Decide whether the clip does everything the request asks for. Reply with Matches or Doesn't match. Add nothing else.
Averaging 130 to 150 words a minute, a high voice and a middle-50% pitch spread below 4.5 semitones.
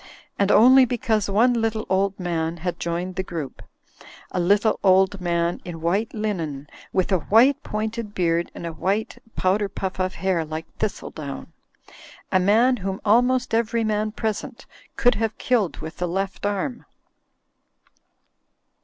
Matches